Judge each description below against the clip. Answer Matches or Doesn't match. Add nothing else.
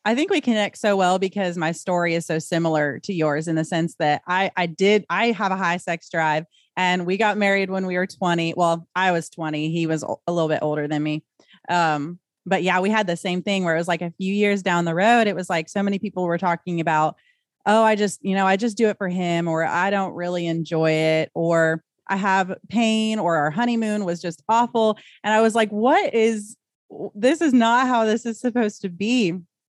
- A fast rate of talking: Matches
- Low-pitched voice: Doesn't match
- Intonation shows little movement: Doesn't match